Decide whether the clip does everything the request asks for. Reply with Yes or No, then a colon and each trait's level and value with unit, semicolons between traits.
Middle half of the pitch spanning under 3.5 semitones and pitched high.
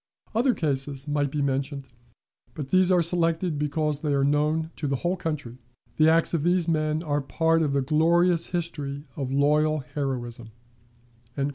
No: average, 2.9 semitones; medium, 150 Hz